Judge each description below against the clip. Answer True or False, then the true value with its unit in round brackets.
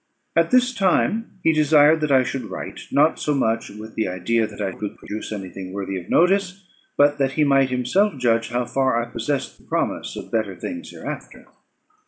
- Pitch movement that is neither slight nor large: False (5.8 semitones)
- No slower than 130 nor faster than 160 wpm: False (200 wpm)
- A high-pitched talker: False (130 Hz)